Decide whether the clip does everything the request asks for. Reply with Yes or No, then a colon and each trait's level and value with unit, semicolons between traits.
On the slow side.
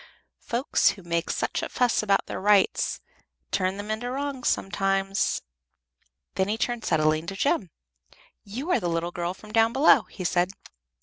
No: average, 165 wpm